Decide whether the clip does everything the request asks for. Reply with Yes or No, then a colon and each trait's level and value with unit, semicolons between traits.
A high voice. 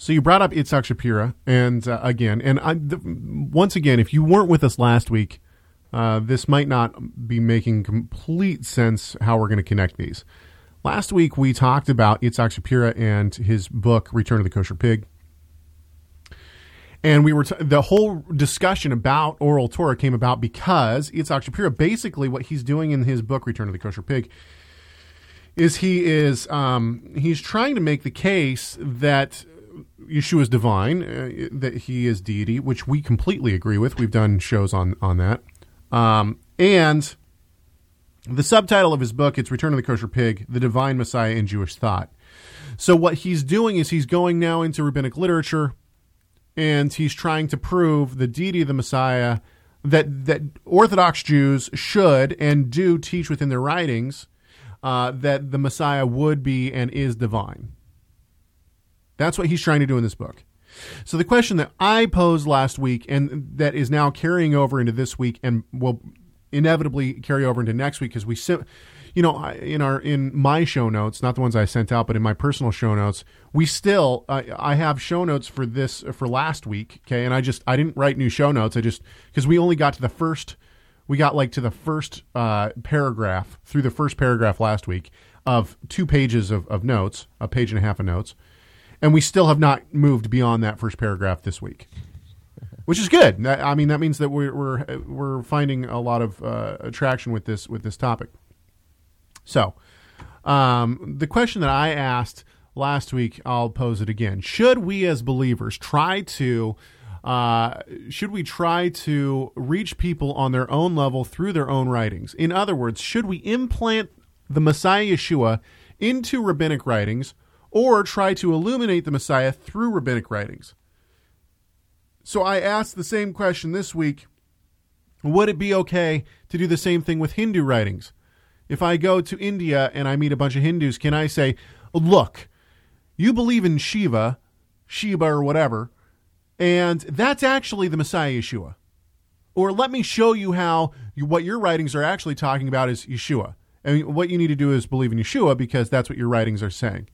No: low, 130 Hz